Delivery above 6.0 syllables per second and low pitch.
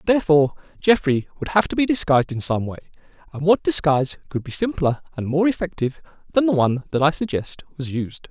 No: 6.4 syllables/s; medium, 160 Hz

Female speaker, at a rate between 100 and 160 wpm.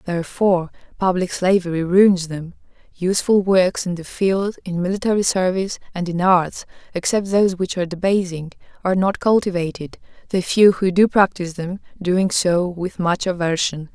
Yes: female; average, 150 wpm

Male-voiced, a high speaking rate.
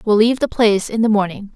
No: female; fast, 270 wpm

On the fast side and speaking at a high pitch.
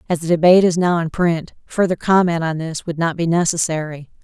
No: fast, 215 wpm; medium, 170 Hz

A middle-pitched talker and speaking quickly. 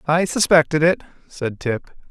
No: medium, 155 Hz; average, 145 wpm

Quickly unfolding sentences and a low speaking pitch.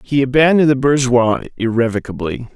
No: slow, 120 wpm; low, 125 Hz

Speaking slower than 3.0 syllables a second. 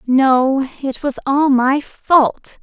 Yes: 2.7 syllables/s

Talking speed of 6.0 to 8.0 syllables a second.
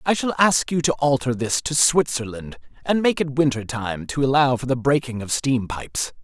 No: 5.0 syllables/s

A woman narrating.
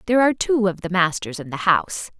Yes: female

